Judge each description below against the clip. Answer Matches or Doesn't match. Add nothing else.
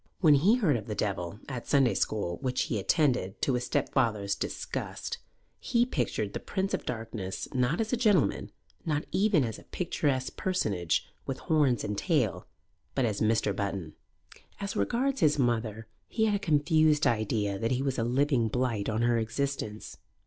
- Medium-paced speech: Matches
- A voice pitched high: Doesn't match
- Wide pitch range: Matches